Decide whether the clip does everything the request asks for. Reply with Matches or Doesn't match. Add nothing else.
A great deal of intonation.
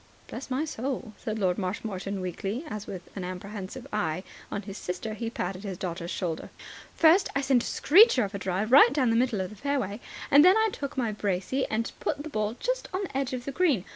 Matches